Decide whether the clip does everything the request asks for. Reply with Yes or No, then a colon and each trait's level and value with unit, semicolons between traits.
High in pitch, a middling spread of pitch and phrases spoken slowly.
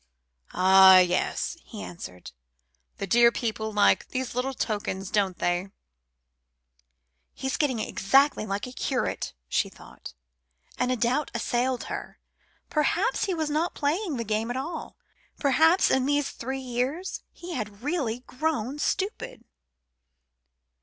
No: very high, 250 Hz; wide, 5.7 semitones; slow, 130 wpm